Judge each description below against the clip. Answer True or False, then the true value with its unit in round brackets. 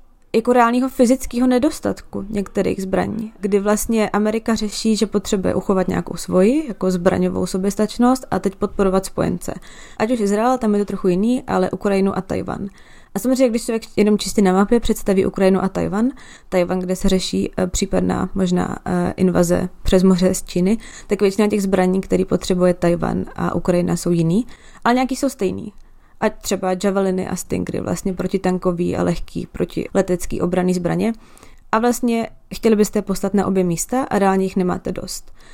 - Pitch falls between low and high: False (195 Hz)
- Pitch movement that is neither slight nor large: True (3.0 semitones)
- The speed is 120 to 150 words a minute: False (165 wpm)